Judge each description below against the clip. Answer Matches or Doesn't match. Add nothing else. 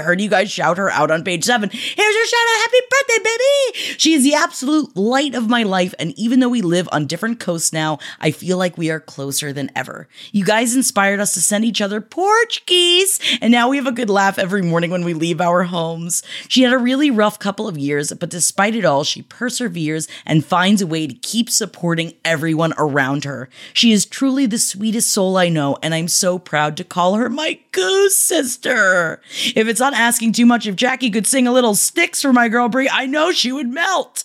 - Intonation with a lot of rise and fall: Matches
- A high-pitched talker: Matches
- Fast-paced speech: Matches